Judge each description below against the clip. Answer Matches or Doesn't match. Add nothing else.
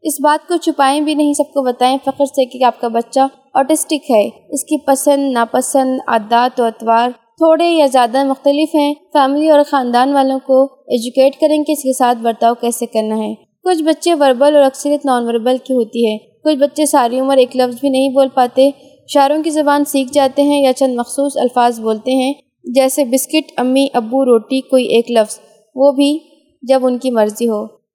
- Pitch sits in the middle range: Doesn't match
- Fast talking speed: Matches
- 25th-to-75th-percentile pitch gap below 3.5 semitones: Matches